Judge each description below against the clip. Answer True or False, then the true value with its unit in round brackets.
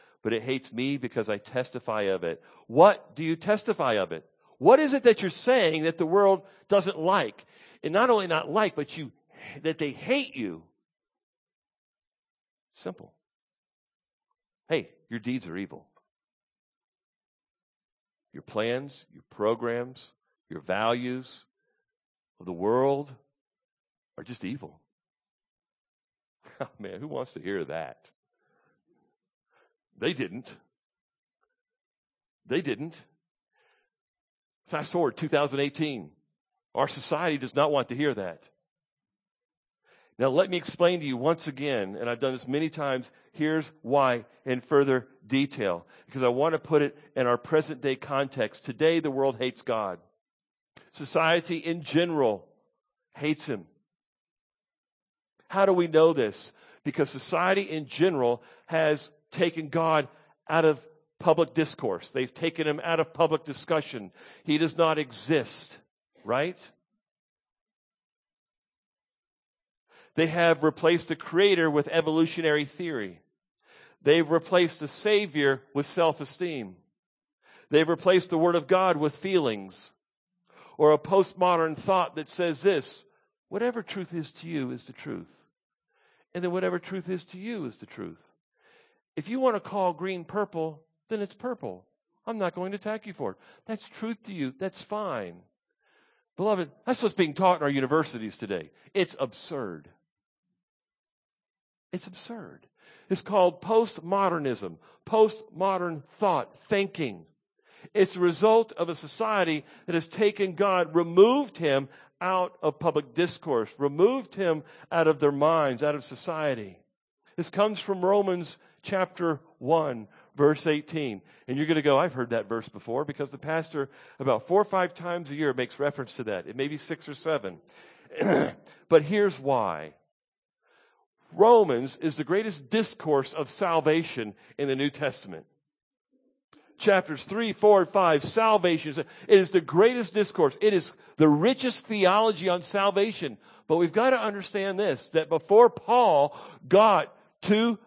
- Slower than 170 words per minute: True (140 wpm)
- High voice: False (165 Hz)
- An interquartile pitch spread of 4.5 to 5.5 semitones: True (5.2 semitones)